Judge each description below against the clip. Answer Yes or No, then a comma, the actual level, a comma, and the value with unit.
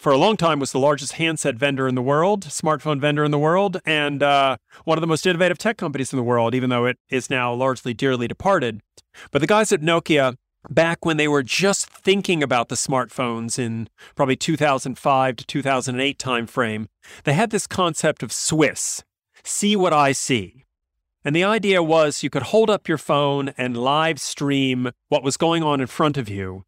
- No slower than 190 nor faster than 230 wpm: Yes, average, 200 wpm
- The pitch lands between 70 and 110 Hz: No, medium, 140 Hz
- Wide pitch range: No, average, 4.3 semitones